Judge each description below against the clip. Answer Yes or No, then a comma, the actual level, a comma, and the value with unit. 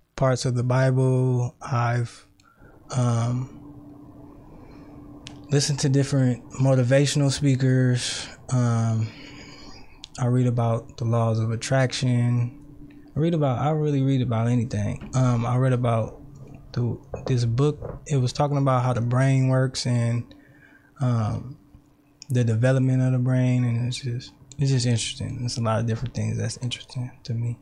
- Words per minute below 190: Yes, average, 140 wpm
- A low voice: Yes, low, 130 Hz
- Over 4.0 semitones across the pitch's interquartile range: No, average, 2.7 semitones